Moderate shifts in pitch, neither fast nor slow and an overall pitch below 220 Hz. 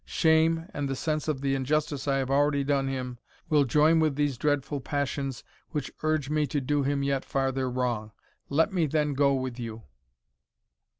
No: narrow, 2.1 semitones; average, 180 wpm; medium, 140 Hz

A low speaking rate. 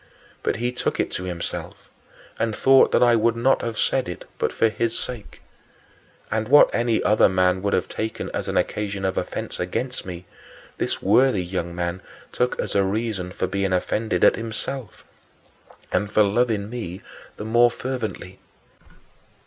No: average, 165 wpm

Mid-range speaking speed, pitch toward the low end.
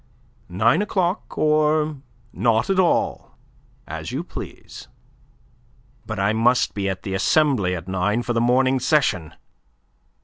No: slow, 130 wpm; low, 120 Hz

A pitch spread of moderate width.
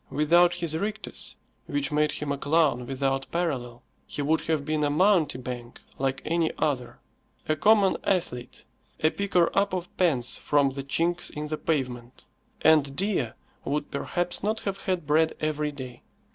Yes: average, 4.2 semitones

